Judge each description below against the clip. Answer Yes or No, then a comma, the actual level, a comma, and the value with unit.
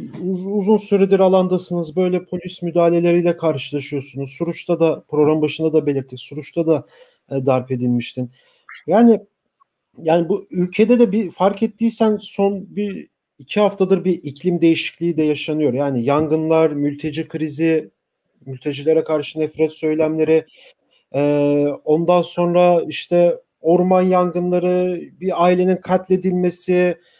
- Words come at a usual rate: No, slow, 115 wpm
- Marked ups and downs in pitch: No, average, 3.1 semitones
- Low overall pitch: No, medium, 170 Hz